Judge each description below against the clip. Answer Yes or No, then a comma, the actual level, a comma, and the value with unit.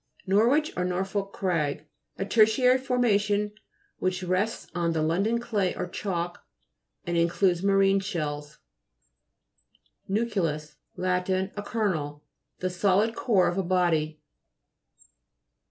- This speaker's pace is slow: Yes, slow, 120 wpm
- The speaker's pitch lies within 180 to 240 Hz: Yes, high, 190 Hz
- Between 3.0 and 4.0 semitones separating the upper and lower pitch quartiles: Yes, average, 3.3 semitones